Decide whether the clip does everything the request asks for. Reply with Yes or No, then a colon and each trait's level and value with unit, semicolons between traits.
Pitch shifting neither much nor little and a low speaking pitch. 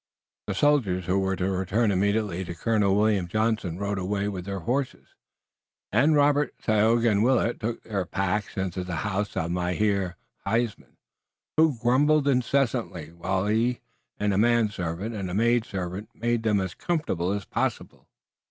Yes: average, 3.9 semitones; low, 105 Hz